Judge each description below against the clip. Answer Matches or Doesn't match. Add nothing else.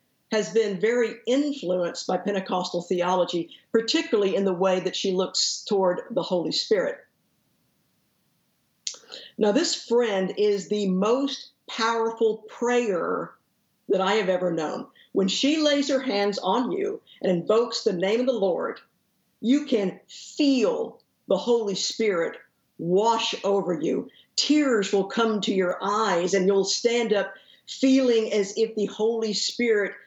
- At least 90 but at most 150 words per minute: Matches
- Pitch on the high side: Matches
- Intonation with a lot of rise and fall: Doesn't match